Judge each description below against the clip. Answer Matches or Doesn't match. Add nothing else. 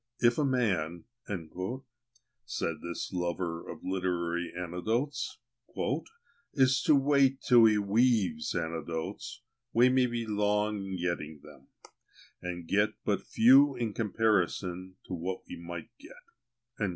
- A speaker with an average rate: Doesn't match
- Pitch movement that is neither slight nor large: Doesn't match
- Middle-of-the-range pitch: Doesn't match